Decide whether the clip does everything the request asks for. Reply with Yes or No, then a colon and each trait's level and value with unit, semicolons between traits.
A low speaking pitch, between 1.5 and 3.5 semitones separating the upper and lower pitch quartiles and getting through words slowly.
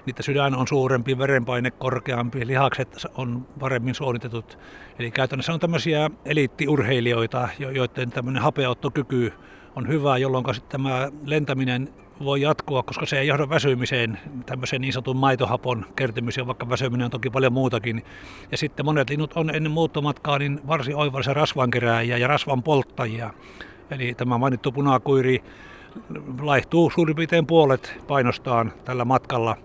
No: low, 130 Hz; narrow, 2.5 semitones; average, 135 wpm